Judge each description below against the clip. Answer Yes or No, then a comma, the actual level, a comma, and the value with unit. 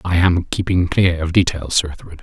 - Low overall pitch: Yes, very low, 85 Hz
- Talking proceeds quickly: Yes, fast, 215 wpm